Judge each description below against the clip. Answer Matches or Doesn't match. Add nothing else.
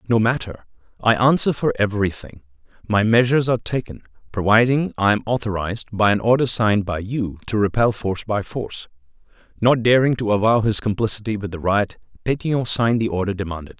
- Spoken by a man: Matches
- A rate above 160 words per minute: Matches